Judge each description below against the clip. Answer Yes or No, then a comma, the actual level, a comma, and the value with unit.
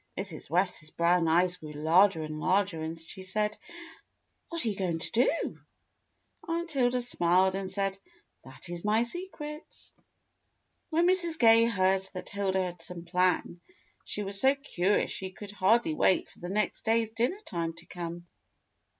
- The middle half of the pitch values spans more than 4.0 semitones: Yes, average, 4.8 semitones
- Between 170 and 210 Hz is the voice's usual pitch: Yes, high, 190 Hz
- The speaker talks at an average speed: Yes, average, 160 wpm